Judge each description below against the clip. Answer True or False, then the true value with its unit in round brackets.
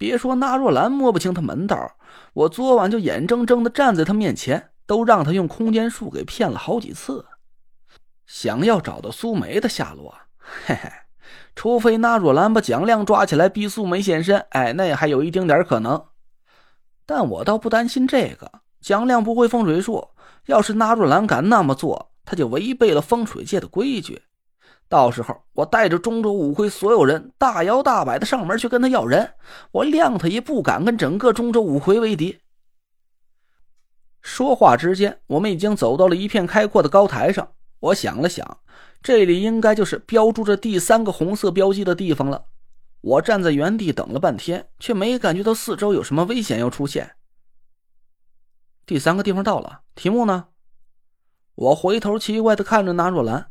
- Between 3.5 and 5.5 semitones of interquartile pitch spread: True (5.1 semitones)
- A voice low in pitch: False (210 Hz)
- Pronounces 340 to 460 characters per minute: False (265 characters per minute)